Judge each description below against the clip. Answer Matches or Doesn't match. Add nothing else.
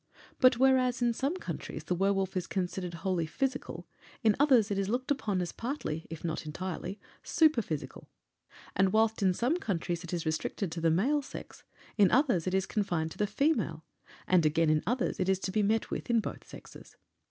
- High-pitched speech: Matches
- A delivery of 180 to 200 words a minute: Matches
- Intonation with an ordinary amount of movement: Doesn't match